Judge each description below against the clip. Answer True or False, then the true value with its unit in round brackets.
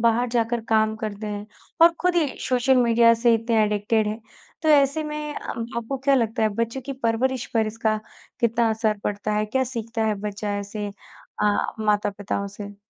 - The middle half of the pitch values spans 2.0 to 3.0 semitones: True (2.7 semitones)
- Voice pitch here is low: False (225 Hz)